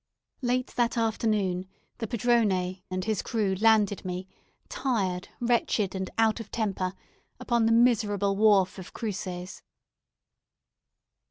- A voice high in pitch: Yes, high, 210 Hz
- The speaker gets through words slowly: Yes, slow, 115 wpm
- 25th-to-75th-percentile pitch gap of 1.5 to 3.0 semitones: No, average, 3.5 semitones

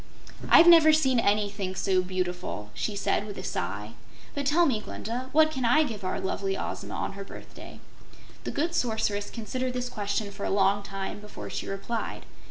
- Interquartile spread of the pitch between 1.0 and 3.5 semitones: No, average, 4.6 semitones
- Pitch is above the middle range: Yes, high, 210 Hz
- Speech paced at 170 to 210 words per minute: Yes, average, 180 wpm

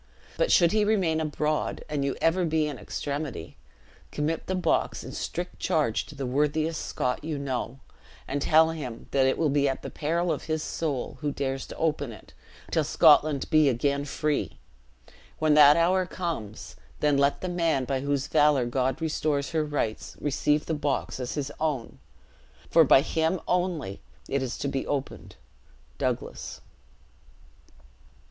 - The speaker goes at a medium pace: Yes, average, 165 wpm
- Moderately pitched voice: Yes, medium, 150 Hz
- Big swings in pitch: No, average, 2.7 semitones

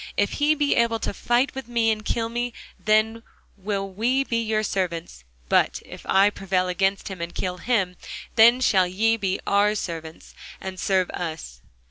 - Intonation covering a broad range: No, average, 3.7 semitones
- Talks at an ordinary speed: Yes, average, 180 wpm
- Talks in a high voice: Yes, high, 205 Hz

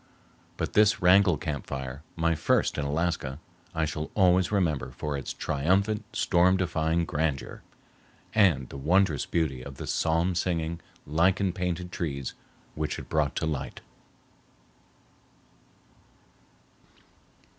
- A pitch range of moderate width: Yes, average, 3.7 semitones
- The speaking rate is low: Yes, slow, 120 wpm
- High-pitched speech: No, very low, 80 Hz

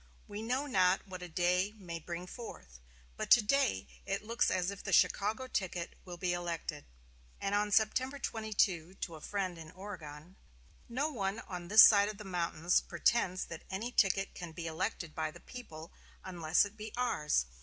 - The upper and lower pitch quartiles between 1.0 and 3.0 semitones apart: No, average, 3.8 semitones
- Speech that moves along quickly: No, average, 180 wpm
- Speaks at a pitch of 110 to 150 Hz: No, medium, 185 Hz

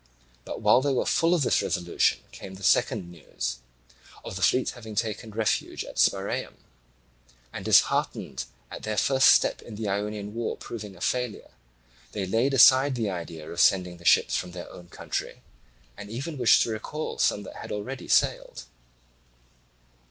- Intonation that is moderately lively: Yes, average, 4.9 semitones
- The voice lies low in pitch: Yes, low, 105 Hz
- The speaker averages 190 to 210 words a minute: No, average, 165 wpm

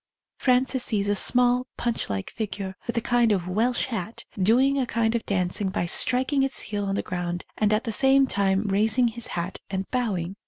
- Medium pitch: No, high, 220 Hz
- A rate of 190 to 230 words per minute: Yes, average, 200 wpm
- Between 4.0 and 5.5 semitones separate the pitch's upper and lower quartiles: Yes, average, 4.3 semitones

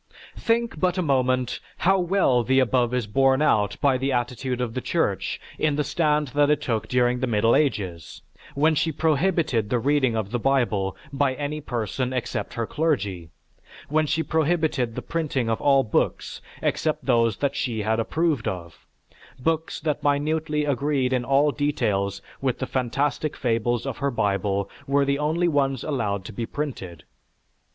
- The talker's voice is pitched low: Yes, low, 130 Hz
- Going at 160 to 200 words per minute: Yes, average, 165 wpm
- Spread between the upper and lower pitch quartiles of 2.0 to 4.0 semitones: No, average, 4.5 semitones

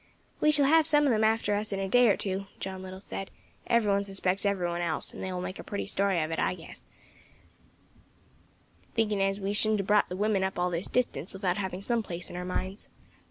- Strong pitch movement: No, narrow, 2.5 semitones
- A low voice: No, high, 195 Hz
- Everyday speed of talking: No, fast, 235 wpm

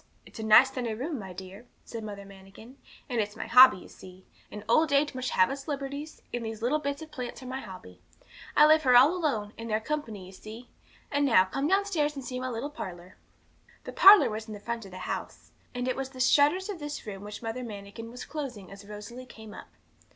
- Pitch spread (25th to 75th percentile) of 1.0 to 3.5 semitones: No, average, 5.2 semitones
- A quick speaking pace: Yes, fast, 230 wpm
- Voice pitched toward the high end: Yes, high, 245 Hz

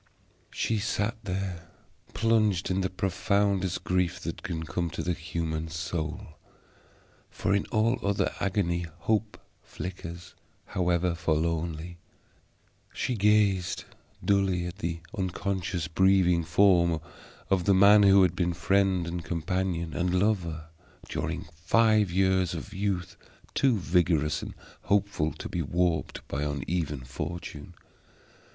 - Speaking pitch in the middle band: No, very low, 90 Hz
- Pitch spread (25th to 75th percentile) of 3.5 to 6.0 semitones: No, average, 2.7 semitones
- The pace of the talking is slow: Yes, slow, 120 wpm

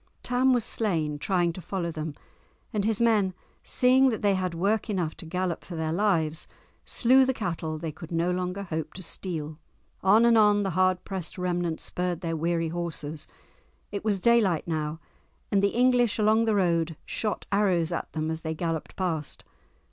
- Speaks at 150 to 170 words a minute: No, average, 180 wpm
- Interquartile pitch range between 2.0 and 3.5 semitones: No, average, 4.2 semitones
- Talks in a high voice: No, medium, 180 Hz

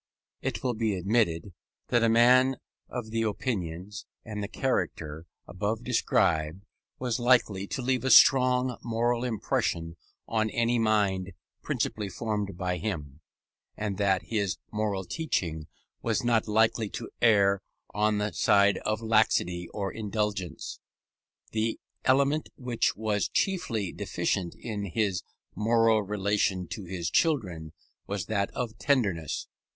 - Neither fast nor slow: No, slow, 130 wpm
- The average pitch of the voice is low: Yes, low, 105 Hz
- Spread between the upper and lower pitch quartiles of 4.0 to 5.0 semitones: No, average, 3.4 semitones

